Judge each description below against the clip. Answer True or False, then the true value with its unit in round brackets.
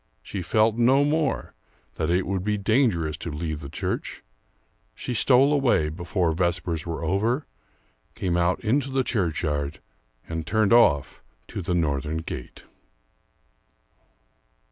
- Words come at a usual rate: False (130 wpm)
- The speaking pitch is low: True (90 Hz)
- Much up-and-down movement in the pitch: True (6.5 semitones)